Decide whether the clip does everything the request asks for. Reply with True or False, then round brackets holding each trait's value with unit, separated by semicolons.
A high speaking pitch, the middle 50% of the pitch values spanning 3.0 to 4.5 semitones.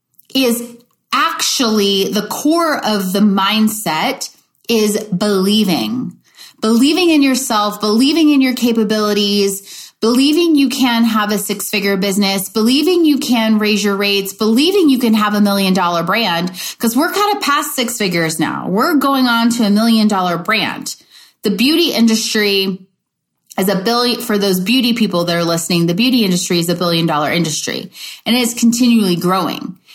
True (215 Hz; 3.9 semitones)